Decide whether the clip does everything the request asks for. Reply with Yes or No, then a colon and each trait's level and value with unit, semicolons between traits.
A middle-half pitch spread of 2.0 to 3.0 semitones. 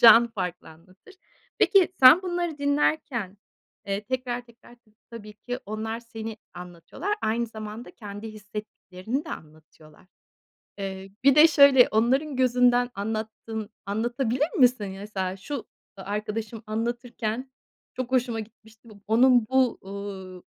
No: average, 3.7 semitones